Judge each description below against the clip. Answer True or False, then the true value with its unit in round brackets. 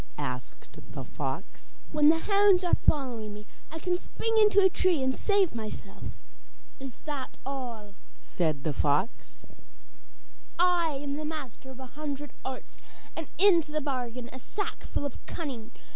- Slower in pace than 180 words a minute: True (150 wpm)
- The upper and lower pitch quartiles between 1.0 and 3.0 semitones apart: False (5.6 semitones)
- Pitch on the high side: True (285 Hz)